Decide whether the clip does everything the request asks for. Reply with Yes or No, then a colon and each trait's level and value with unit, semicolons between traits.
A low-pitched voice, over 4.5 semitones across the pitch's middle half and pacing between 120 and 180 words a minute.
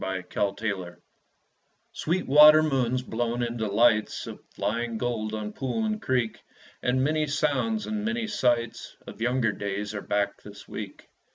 Yes: low, 120 Hz; wide, 5.5 semitones; average, 150 wpm